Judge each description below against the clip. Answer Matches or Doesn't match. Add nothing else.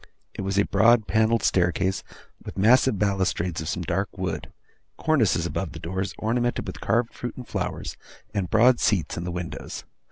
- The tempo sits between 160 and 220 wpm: Matches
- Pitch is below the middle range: Matches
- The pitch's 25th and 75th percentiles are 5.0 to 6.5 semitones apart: Doesn't match